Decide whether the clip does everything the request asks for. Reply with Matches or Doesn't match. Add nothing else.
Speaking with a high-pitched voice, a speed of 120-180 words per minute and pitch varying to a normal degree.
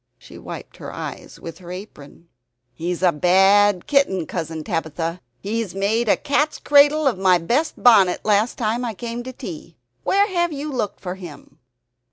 Doesn't match